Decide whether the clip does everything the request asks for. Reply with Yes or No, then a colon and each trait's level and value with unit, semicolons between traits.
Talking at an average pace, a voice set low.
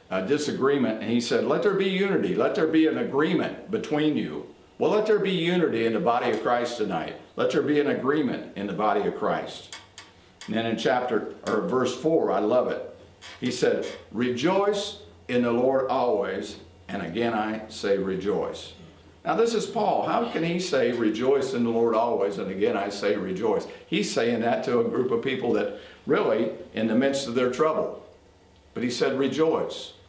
No: average, 195 wpm; medium, 145 Hz